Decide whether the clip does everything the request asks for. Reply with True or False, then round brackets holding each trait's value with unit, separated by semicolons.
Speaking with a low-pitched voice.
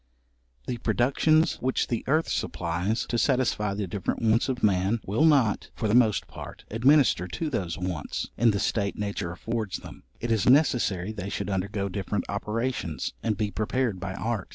True (105 Hz)